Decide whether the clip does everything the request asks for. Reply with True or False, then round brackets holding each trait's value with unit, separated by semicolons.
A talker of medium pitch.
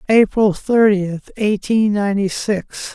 False (205 Hz)